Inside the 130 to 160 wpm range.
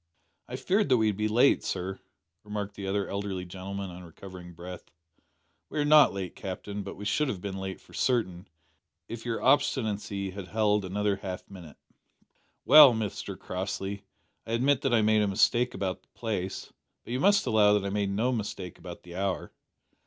No: average, 180 wpm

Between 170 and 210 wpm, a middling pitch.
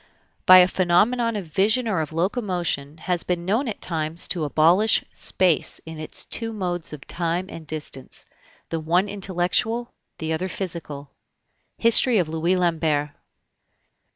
No: average, 145 wpm; medium, 175 Hz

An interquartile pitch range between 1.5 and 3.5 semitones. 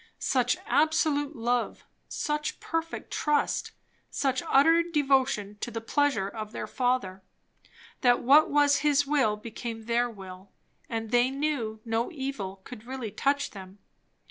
No: average, 4.6 semitones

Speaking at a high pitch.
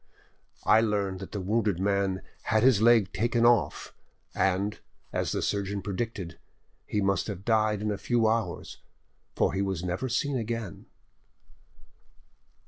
No: low, 105 Hz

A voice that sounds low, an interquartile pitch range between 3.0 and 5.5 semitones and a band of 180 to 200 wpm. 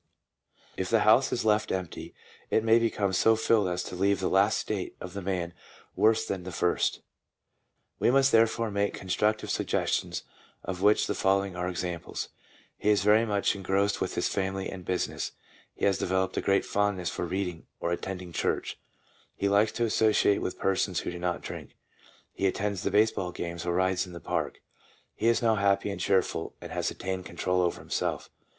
No: very low, 95 Hz; narrow, 2.5 semitones; average, 190 wpm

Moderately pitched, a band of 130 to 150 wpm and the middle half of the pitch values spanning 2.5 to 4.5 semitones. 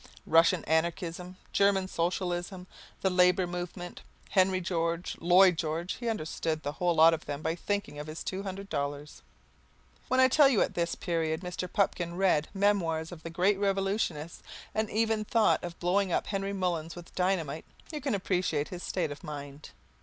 No: medium, 180 Hz; average, 175 wpm; average, 3.0 semitones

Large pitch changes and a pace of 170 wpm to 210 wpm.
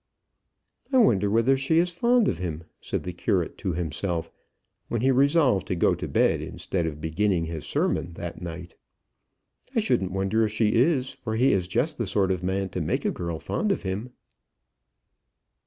Yes: wide, 6.9 semitones; average, 185 wpm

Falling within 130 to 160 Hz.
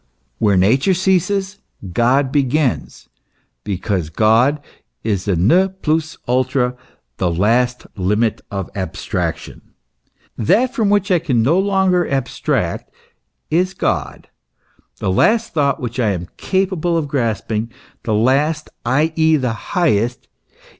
Yes: low, 135 Hz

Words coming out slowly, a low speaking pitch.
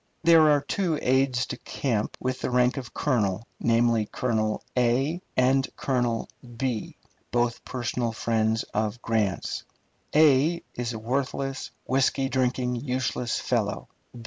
Yes: slow, 115 wpm; low, 125 Hz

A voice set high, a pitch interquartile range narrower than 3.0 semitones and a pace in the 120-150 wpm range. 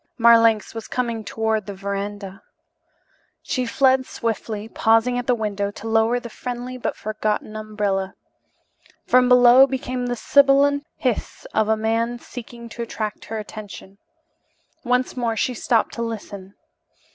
Yes: high, 225 Hz; narrow, 2.5 semitones; average, 140 wpm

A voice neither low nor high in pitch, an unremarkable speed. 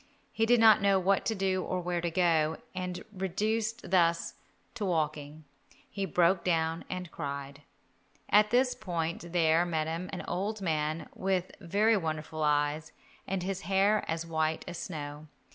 Yes: medium, 175 Hz; average, 155 wpm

